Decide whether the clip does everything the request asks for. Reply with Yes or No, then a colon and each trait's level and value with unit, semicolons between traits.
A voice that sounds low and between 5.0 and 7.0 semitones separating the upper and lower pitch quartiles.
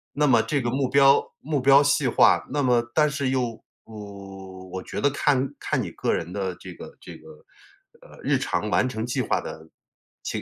Yes: low, 130 Hz; wide, 5.6 semitones